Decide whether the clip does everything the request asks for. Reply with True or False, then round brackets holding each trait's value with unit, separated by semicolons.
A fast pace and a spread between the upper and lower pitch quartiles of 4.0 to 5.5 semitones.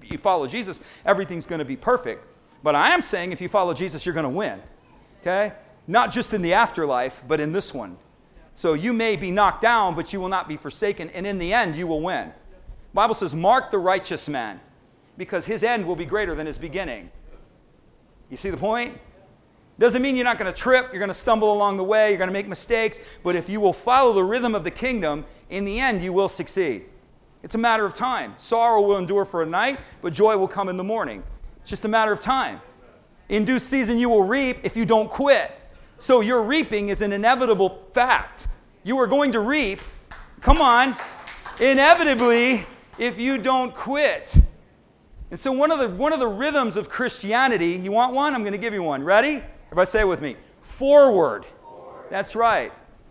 True (210 wpm; 4.8 semitones)